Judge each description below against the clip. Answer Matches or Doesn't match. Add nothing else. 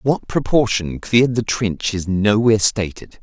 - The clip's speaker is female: Doesn't match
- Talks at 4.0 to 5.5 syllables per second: Matches